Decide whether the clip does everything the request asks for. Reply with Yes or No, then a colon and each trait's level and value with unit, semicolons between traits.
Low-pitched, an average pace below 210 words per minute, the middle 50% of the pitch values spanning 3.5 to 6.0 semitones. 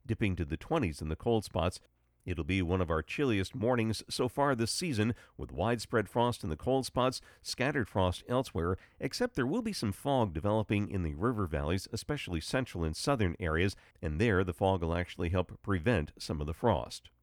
Yes: low, 100 Hz; average, 200 wpm; average, 5.2 semitones